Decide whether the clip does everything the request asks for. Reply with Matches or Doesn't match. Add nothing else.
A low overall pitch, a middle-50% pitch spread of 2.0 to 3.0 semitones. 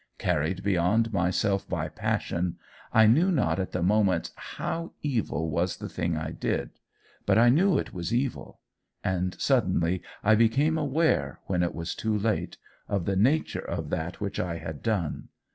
Doesn't match